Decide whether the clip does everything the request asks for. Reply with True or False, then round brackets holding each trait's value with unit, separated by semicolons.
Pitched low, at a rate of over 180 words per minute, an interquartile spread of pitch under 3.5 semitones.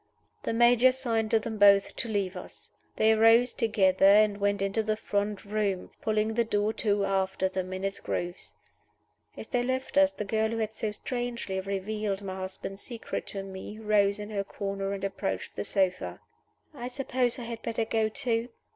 False (210 Hz; 190 wpm; 2.5 semitones)